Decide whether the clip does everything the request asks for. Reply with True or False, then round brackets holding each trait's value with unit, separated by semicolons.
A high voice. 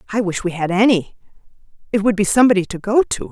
True (205 Hz)